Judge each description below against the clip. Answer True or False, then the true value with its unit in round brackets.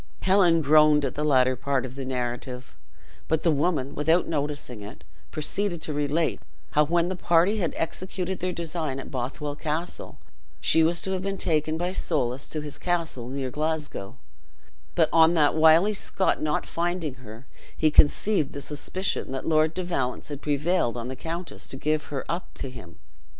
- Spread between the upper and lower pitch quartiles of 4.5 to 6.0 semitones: False (4.0 semitones)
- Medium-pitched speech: True (155 Hz)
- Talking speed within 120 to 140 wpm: False (175 wpm)